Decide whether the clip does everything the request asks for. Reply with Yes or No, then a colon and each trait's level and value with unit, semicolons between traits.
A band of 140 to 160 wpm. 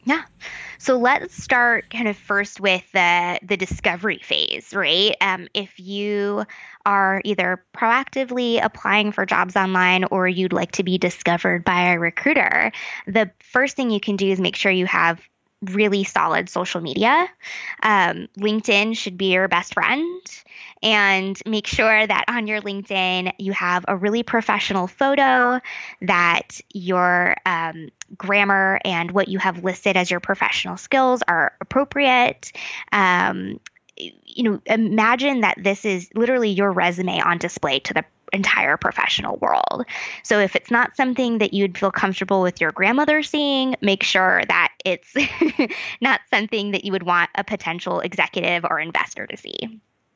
Yes: average, 155 wpm